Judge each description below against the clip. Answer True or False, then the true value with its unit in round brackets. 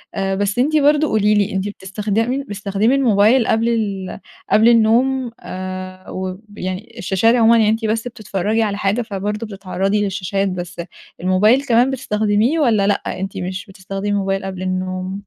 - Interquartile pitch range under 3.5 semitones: True (3.0 semitones)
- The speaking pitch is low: False (205 Hz)